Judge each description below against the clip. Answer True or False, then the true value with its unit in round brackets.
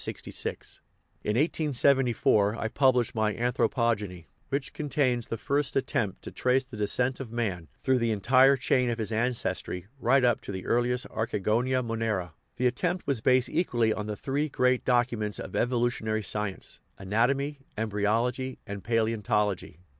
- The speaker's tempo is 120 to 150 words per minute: True (145 wpm)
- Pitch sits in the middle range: False (120 Hz)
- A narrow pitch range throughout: False (3.2 semitones)